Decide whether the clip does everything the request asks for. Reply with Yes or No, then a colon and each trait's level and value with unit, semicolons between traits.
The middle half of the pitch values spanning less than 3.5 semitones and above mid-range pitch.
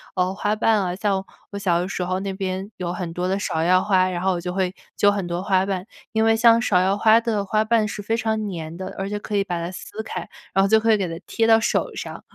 Yes: average, 2.8 semitones; high, 195 Hz